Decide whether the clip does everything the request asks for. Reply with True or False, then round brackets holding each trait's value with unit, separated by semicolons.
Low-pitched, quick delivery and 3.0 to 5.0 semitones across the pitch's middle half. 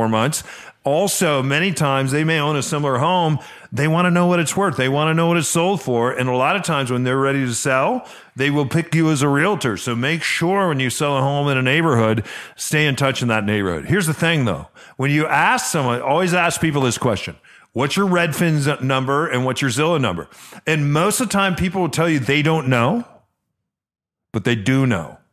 False (145 Hz; 230 wpm; 4.5 semitones)